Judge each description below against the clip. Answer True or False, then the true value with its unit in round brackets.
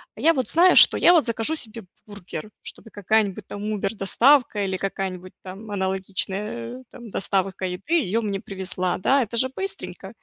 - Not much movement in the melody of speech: False (3.6 semitones)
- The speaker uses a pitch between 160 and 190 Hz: False (205 Hz)